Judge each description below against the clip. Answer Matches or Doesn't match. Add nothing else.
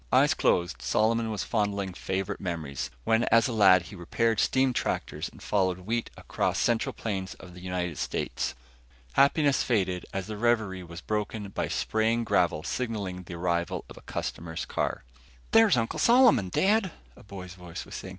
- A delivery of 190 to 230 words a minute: Doesn't match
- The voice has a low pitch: Matches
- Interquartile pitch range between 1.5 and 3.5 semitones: Doesn't match